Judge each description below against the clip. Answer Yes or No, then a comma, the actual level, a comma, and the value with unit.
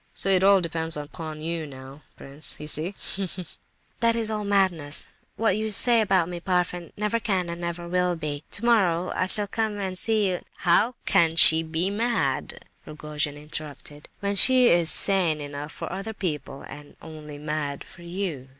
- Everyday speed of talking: Yes, average, 175 wpm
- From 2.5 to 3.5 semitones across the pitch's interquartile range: No, average, 4.6 semitones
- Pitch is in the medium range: Yes, medium, 175 Hz